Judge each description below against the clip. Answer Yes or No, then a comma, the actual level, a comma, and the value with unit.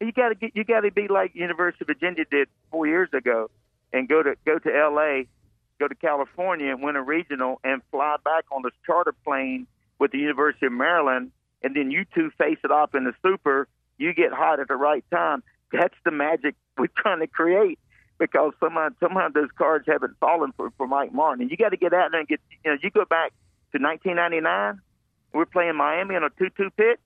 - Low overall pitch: No, medium, 150 Hz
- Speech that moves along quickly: Yes, fast, 220 wpm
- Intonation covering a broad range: No, average, 4.8 semitones